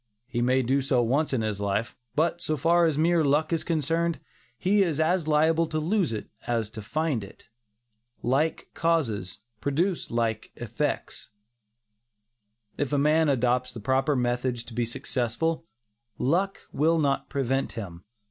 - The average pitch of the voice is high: No, medium, 140 Hz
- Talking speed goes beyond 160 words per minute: No, average, 155 wpm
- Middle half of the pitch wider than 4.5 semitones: Yes, average, 5.2 semitones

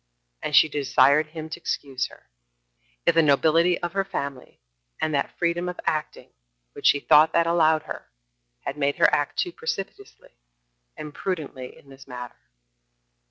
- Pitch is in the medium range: Yes, medium, 155 Hz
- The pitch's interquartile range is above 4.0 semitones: No, average, 3.2 semitones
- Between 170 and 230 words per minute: No, average, 160 wpm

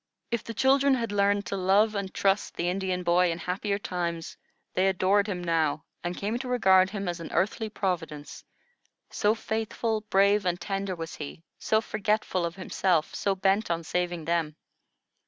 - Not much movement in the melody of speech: No, average, 3.1 semitones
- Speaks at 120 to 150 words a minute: No, average, 175 wpm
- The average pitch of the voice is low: No, high, 190 Hz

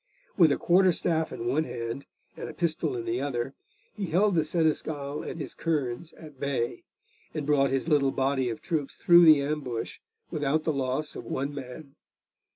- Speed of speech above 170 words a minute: Yes, average, 180 wpm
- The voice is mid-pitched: Yes, medium, 145 Hz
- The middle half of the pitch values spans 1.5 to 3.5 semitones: Yes, average, 3.0 semitones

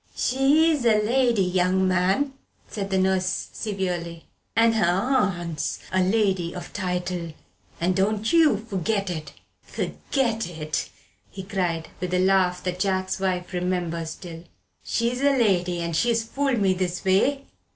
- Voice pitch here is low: No, high, 190 Hz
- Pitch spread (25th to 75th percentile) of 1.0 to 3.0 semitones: No, average, 3.9 semitones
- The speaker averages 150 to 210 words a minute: No, average, 140 wpm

